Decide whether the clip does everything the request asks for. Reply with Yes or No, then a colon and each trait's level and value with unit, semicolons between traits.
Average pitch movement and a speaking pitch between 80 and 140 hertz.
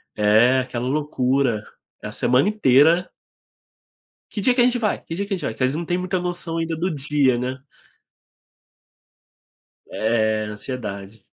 No: wide, 6.6 semitones; low, 135 Hz